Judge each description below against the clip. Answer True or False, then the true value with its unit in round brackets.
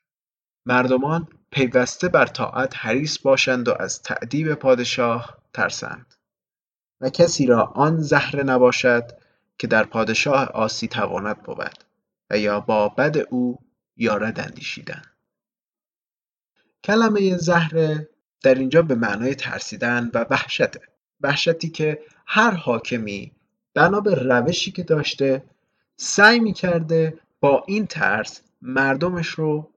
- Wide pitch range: False (5.0 semitones)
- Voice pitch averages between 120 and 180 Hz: True (140 Hz)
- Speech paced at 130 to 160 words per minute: False (110 wpm)